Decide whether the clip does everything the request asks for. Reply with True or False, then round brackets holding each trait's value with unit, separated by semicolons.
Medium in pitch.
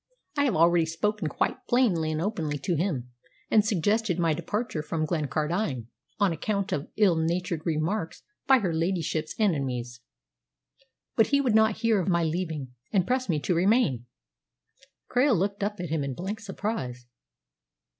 True (175 Hz)